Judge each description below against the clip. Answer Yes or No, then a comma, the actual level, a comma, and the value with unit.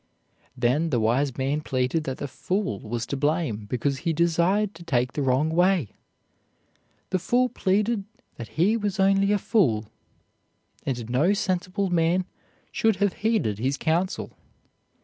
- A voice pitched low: No, medium, 165 Hz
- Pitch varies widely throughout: Yes, wide, 6.9 semitones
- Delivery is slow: No, average, 150 wpm